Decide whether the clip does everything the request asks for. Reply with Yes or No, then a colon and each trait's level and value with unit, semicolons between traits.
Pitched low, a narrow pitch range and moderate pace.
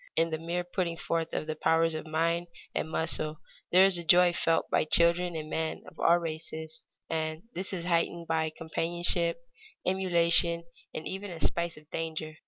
No: medium, 165 Hz; narrow, 1.4 semitones; average, 185 wpm